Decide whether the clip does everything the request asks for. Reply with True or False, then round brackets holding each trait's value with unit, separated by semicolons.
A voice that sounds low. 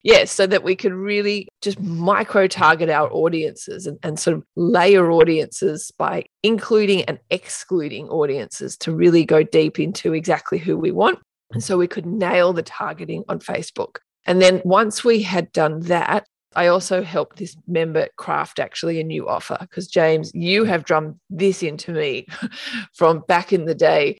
False (180 Hz)